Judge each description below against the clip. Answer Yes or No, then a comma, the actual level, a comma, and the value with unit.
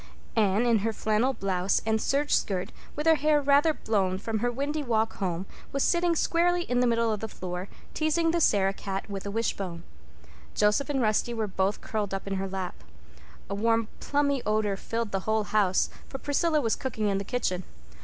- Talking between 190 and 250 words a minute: Yes, average, 195 wpm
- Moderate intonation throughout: No, wide, 6.0 semitones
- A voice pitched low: No, high, 220 Hz